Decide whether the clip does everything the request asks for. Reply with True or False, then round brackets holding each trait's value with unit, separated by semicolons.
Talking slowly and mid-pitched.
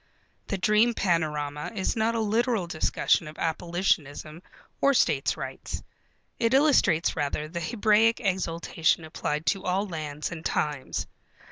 True (130 wpm; 175 Hz)